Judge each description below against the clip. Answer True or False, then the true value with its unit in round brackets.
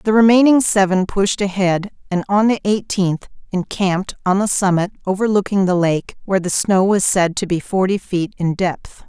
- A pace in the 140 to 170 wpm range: False (180 wpm)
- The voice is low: False (190 Hz)